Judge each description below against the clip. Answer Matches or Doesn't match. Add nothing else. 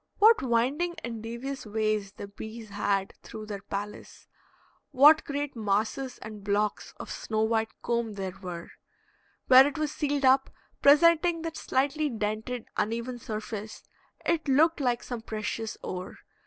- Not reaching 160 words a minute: Matches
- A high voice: Matches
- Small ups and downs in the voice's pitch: Doesn't match